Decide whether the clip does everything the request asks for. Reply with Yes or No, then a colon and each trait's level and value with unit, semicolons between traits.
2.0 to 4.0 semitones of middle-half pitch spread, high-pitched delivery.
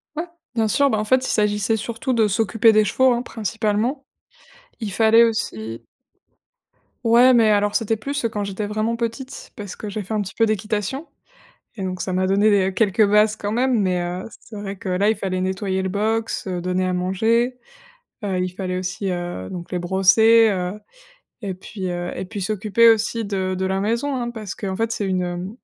Yes: average, 3.2 semitones; high, 210 Hz